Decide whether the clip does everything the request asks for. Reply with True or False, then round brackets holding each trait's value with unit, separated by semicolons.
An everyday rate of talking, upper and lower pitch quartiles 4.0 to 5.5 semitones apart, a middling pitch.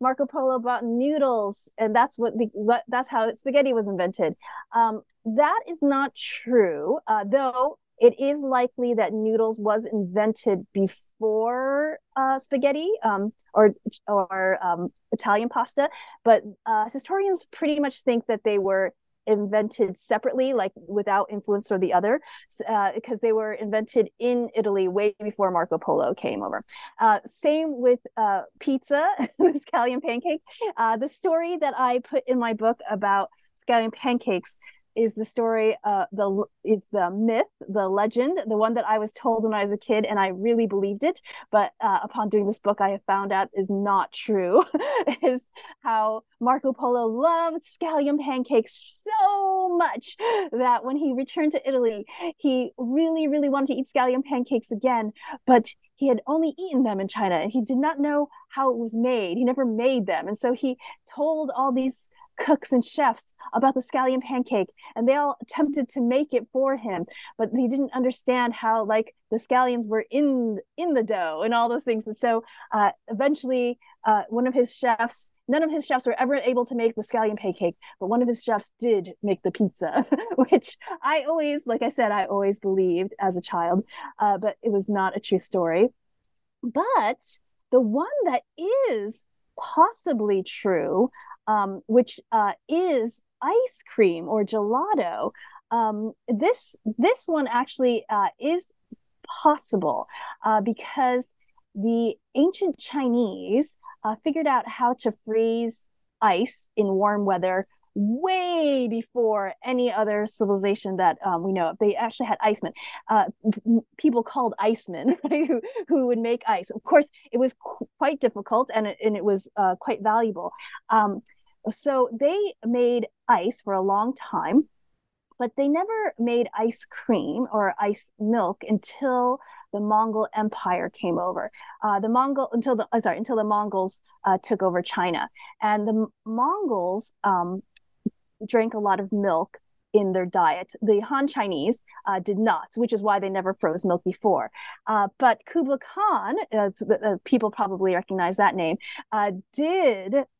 False (160 wpm; 4.6 semitones; 235 Hz)